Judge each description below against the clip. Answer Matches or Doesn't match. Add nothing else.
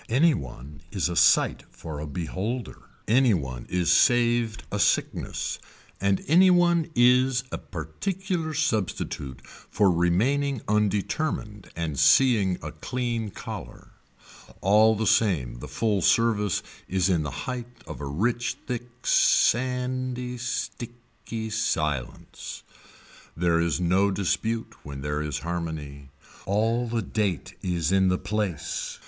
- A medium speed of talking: Doesn't match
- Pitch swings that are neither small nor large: Doesn't match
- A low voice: Matches